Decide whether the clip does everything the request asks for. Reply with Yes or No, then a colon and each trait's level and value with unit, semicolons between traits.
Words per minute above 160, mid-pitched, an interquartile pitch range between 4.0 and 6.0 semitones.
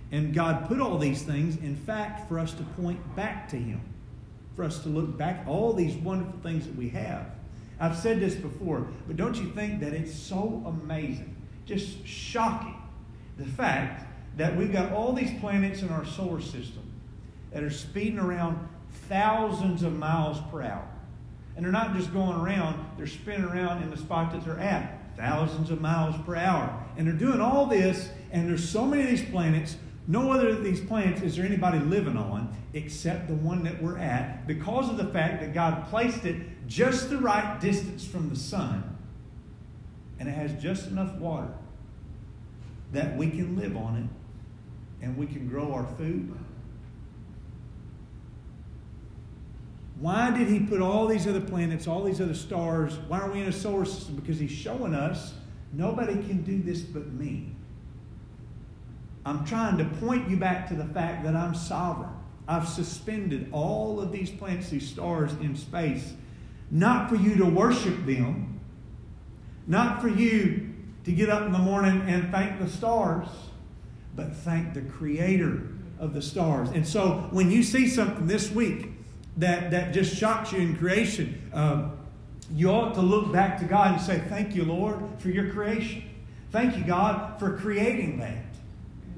Yes: average, 175 wpm; medium, 170 Hz; average, 4.8 semitones